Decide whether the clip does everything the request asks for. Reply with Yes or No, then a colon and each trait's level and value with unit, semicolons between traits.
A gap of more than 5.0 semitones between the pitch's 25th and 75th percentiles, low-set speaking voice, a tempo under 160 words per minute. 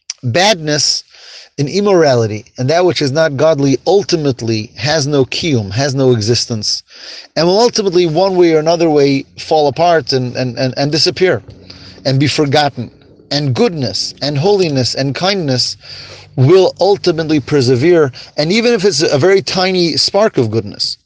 No: wide, 5.5 semitones; medium, 145 Hz; average, 150 wpm